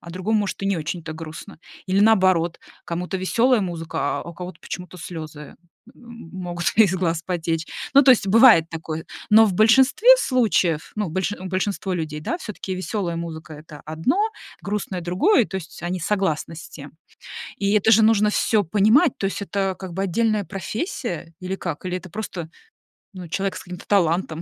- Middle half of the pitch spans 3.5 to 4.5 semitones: Yes, average, 3.9 semitones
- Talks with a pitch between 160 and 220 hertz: Yes, medium, 185 Hz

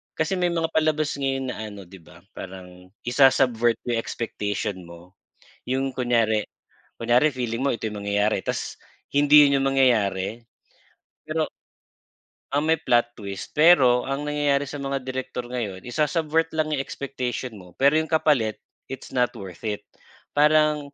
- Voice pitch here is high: No, low, 130 Hz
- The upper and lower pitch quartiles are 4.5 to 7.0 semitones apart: Yes, average, 5.2 semitones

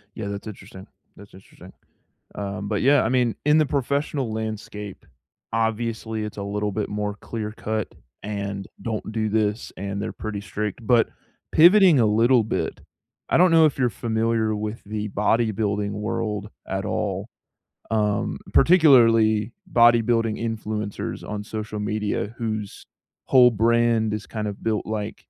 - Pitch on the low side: Yes, low, 110 Hz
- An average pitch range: No, narrow, 1.9 semitones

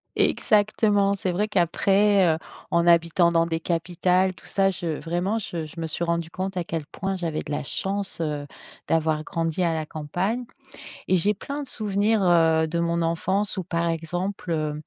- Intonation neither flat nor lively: Yes, average, 3.0 semitones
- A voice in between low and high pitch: Yes, medium, 175 Hz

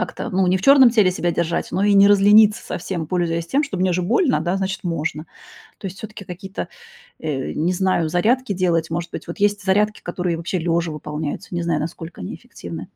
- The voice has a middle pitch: Yes, medium, 180 Hz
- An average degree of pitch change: Yes, average, 3.2 semitones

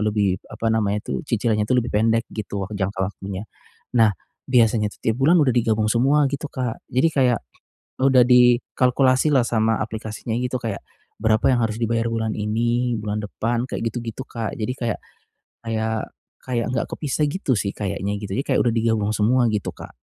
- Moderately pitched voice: No, low, 115 Hz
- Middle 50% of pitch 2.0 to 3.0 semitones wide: Yes, narrow, 2.6 semitones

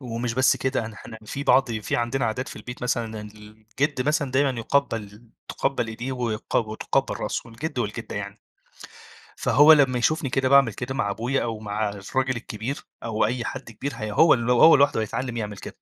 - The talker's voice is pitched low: Yes, low, 120 Hz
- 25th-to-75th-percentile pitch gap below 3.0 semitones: No, average, 3.5 semitones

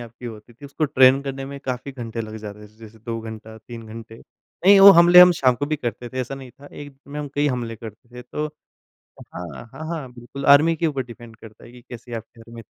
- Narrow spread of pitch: No, average, 3.8 semitones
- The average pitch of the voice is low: Yes, low, 125 Hz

